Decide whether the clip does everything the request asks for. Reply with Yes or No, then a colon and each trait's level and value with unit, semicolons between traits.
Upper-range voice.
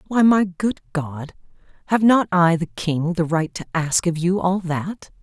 No: medium, 175 Hz